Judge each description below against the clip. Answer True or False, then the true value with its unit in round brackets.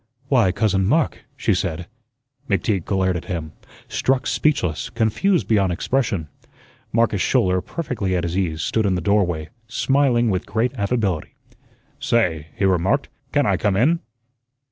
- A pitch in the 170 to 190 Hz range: False (100 Hz)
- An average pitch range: True (4.9 semitones)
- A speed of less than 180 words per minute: True (145 wpm)